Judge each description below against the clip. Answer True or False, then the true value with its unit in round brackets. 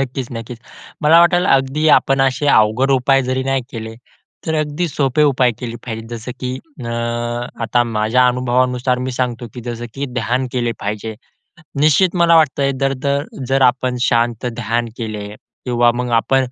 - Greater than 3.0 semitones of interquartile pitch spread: False (2.4 semitones)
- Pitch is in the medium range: False (125 Hz)